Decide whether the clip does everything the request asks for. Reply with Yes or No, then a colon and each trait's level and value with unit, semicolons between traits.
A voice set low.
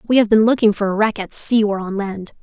No: high, 210 Hz